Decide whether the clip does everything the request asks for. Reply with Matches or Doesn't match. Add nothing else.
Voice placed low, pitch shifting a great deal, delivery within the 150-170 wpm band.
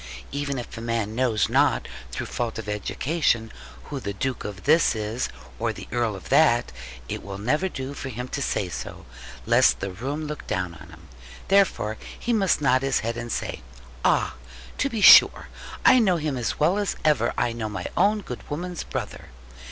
Doesn't match